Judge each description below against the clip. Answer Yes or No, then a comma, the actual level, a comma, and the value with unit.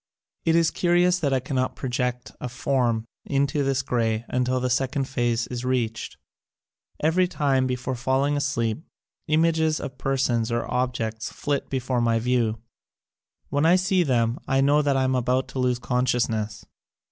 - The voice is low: Yes, low, 130 Hz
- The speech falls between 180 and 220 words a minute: No, average, 165 wpm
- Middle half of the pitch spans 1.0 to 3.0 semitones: Yes, average, 2.7 semitones